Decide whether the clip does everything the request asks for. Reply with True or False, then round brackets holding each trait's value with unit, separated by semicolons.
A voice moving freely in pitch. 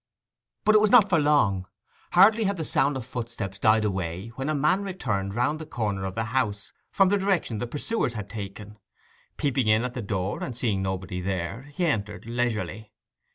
True (6.8 semitones)